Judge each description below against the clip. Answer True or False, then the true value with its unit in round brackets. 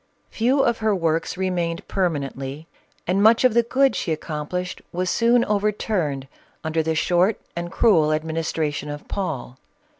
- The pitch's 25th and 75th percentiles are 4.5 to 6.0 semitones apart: True (5.2 semitones)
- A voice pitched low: False (175 Hz)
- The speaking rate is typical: True (155 wpm)